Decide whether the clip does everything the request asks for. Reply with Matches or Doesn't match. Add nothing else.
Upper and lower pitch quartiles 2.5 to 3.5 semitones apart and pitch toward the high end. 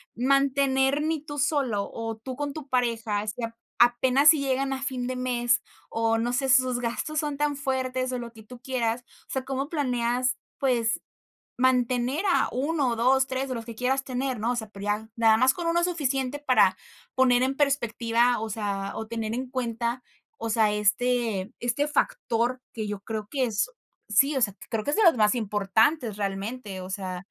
Matches